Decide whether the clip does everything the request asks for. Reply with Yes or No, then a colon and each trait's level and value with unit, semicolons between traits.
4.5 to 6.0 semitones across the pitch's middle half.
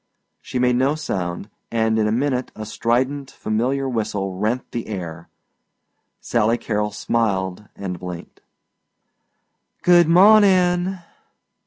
Yes: average, 5.0 semitones